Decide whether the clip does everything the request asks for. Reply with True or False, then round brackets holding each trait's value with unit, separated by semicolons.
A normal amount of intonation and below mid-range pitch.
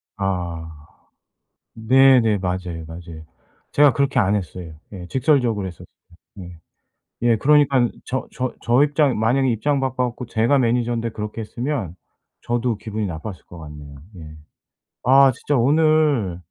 False (6.4 semitones; 115 Hz)